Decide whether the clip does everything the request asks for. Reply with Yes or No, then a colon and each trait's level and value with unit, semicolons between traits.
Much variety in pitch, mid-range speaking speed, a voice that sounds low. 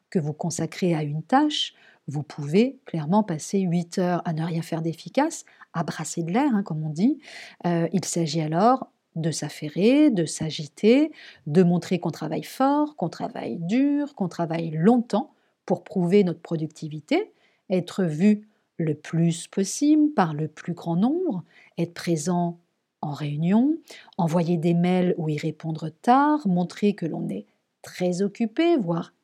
No: wide, 5.7 semitones; average, 155 wpm; medium, 180 Hz